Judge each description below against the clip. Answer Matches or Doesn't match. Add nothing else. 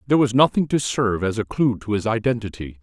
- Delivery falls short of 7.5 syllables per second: Matches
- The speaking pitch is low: Matches